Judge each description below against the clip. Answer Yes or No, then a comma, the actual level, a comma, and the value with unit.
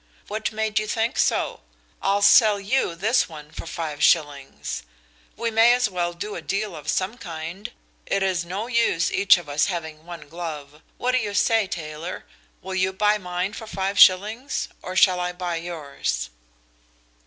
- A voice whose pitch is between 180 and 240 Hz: Yes, medium, 185 Hz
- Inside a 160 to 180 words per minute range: Yes, average, 175 wpm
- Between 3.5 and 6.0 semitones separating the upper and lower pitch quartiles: Yes, average, 4.2 semitones